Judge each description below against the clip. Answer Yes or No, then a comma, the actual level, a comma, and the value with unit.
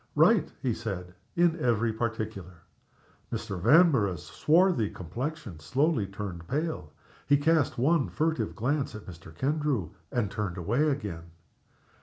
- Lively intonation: Yes, wide, 8.0 semitones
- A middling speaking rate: No, slow, 125 wpm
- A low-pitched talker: Yes, low, 115 Hz